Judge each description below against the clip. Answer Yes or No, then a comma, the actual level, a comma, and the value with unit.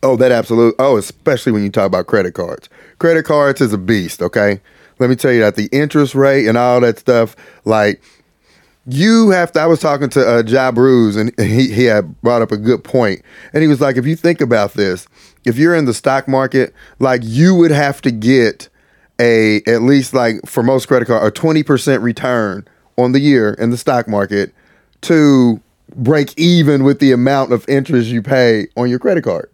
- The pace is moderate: No, fast, 210 wpm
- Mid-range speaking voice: No, low, 130 Hz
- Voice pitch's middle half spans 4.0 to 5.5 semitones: No, average, 3.6 semitones